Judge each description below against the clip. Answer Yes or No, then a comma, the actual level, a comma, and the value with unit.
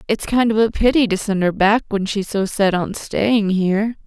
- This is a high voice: Yes, high, 205 Hz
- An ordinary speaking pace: No, fast, 235 wpm